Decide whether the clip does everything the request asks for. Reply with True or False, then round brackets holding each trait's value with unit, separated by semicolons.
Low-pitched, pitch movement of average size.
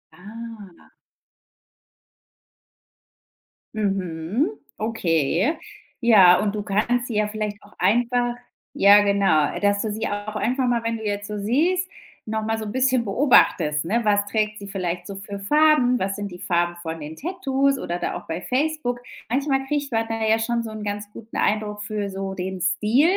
False (215 Hz; 3.5 semitones)